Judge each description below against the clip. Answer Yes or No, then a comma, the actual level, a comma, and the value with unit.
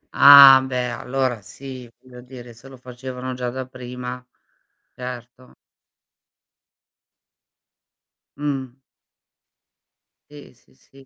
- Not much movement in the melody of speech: Yes, narrow, 1.2 semitones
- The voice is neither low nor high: No, low, 125 Hz